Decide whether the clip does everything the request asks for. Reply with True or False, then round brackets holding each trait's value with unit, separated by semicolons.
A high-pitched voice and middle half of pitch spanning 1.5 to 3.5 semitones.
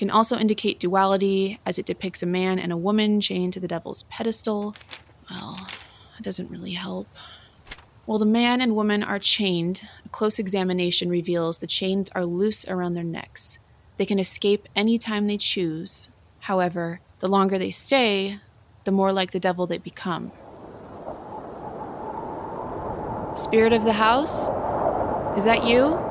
True (195 Hz; 2.9 semitones)